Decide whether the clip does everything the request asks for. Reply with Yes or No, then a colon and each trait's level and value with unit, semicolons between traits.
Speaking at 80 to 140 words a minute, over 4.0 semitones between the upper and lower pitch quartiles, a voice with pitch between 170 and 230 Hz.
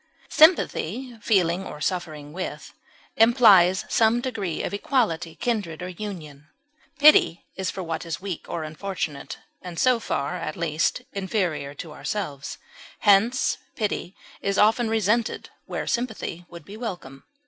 Yes: slow, 135 wpm; average, 5.3 semitones; high, 190 Hz